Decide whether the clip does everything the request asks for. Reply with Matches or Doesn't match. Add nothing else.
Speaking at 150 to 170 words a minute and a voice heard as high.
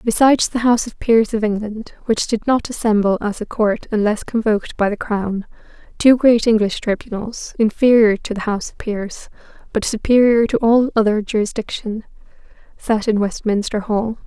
Matches